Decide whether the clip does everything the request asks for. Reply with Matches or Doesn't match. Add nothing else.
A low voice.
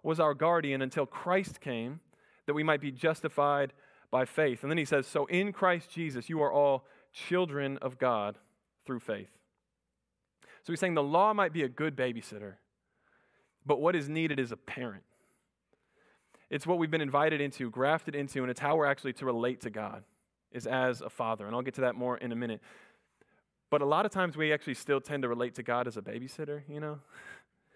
Doesn't match